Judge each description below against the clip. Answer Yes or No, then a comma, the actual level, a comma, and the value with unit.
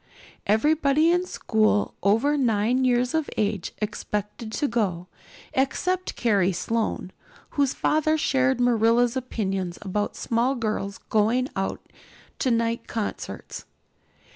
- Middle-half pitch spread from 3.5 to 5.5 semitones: Yes, average, 4.1 semitones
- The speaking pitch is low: No, high, 230 Hz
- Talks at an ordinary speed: No, slow, 115 wpm